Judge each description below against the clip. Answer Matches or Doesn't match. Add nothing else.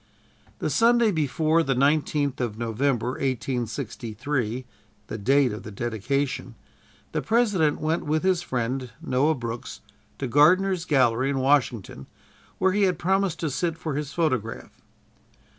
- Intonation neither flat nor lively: Matches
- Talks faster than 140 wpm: Doesn't match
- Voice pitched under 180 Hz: Matches